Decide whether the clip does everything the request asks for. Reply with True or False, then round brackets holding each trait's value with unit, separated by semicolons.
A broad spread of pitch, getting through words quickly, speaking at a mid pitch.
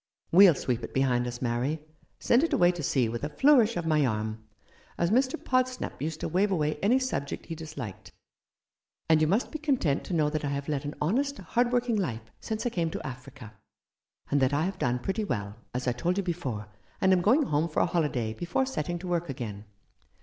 True (7.6 semitones; 230 wpm; 155 Hz)